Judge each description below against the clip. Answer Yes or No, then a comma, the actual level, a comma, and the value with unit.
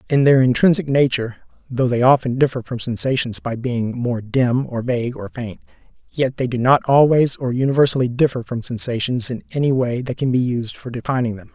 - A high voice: No, low, 125 Hz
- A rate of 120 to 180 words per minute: No, average, 200 wpm